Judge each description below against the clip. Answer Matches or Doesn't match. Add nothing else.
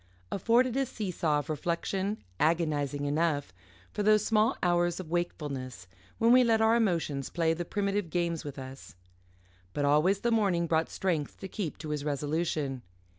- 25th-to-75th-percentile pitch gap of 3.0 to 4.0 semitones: Doesn't match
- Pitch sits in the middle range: Matches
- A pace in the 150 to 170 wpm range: Matches